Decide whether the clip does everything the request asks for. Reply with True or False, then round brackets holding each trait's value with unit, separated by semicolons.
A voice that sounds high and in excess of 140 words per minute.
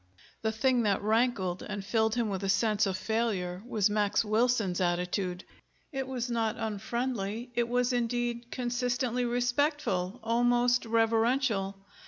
False (230 Hz; 135 wpm)